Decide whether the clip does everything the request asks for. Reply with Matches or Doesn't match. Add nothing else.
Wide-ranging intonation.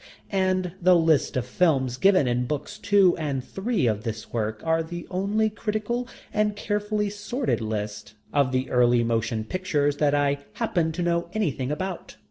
Matches